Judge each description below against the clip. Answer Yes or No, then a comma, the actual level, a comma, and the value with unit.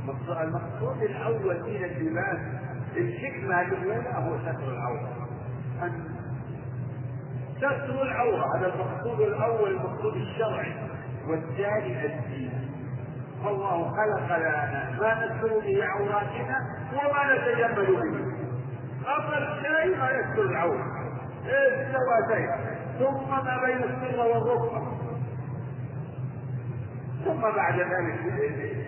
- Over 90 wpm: No, average, 85 wpm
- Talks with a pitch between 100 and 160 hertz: Yes, low, 135 Hz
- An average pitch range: Yes, average, 4.4 semitones